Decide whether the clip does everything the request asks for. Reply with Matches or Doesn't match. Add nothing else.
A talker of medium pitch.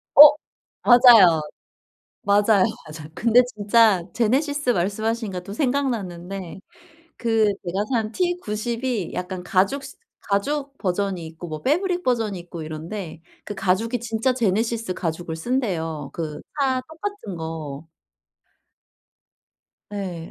Doesn't match